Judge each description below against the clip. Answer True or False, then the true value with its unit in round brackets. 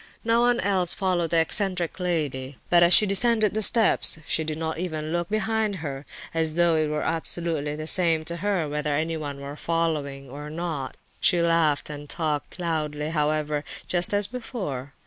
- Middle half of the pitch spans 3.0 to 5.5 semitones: True (3.3 semitones)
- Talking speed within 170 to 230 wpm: True (175 wpm)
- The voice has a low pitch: False (165 Hz)